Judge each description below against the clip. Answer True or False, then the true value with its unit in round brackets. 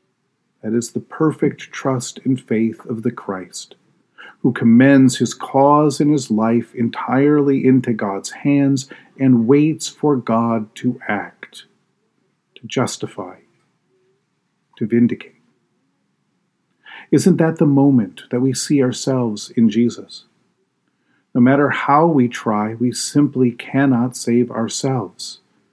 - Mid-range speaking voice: False (130 Hz)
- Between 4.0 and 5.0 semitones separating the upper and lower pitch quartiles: False (3.3 semitones)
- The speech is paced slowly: True (120 wpm)